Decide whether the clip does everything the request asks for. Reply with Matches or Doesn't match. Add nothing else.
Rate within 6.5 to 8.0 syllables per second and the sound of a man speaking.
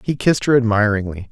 Matches